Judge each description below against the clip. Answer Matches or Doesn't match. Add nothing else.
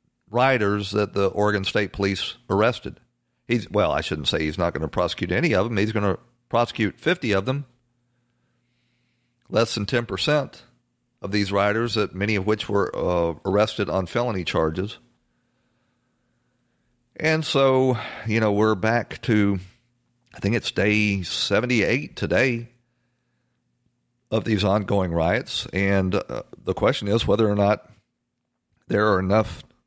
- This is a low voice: Matches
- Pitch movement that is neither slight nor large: Matches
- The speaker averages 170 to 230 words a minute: Doesn't match